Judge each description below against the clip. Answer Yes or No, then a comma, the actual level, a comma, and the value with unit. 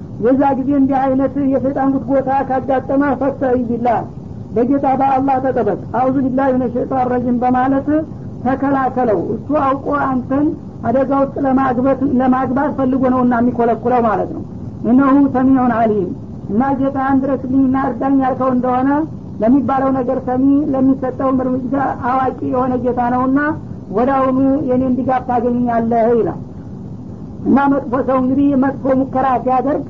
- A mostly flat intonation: Yes, narrow, 1.3 semitones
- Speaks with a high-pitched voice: Yes, very high, 265 Hz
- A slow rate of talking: Yes, slow, 125 wpm